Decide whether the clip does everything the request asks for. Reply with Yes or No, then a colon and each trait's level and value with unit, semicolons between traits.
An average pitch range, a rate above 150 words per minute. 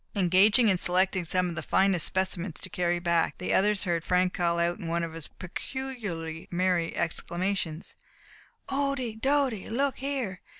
Yes: average, 4.0 semitones; average, 160 wpm